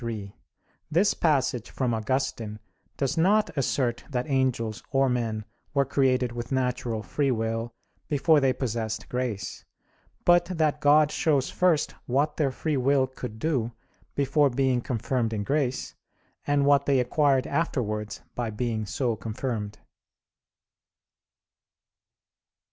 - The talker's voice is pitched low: Yes, low, 130 Hz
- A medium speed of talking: No, slow, 125 wpm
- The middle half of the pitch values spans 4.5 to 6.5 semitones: No, average, 3.7 semitones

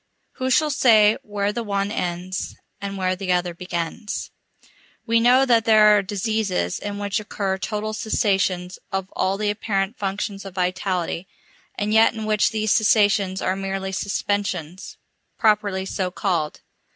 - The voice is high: Yes, high, 200 Hz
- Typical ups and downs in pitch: No, narrow, 2.3 semitones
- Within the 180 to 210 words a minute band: No, average, 150 wpm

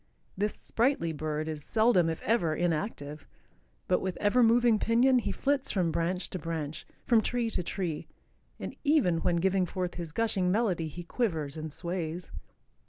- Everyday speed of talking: Yes, average, 165 wpm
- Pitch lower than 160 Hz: No, medium, 180 Hz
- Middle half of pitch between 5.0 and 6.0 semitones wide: Yes, wide, 5.6 semitones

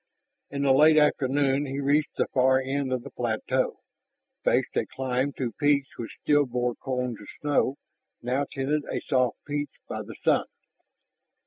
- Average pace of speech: Yes, average, 160 wpm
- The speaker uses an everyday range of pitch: No, narrow, 2.1 semitones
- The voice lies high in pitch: No, low, 135 Hz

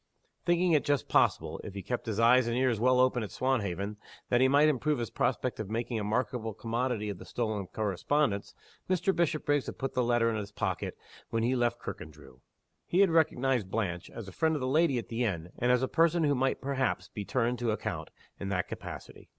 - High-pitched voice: No, low, 120 Hz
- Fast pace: Yes, fast, 215 wpm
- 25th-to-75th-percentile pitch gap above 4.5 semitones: No, average, 4.1 semitones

